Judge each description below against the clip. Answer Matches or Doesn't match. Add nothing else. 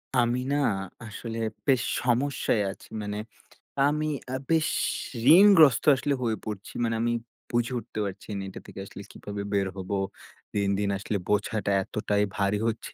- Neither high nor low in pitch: Doesn't match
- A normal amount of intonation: Matches